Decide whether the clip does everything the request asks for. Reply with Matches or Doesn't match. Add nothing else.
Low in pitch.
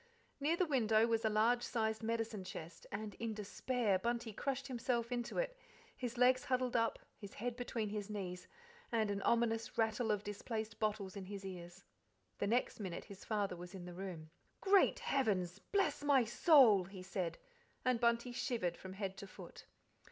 Doesn't match